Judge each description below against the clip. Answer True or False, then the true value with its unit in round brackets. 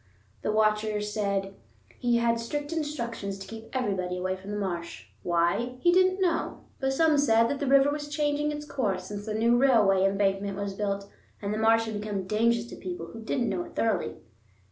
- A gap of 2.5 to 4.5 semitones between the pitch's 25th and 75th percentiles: False (5.2 semitones)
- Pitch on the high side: True (220 Hz)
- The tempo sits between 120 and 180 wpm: False (195 wpm)